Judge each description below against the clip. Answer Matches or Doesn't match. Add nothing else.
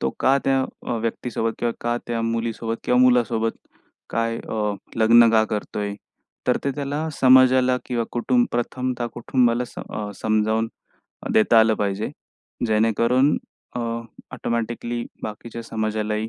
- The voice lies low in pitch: Matches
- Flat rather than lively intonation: Matches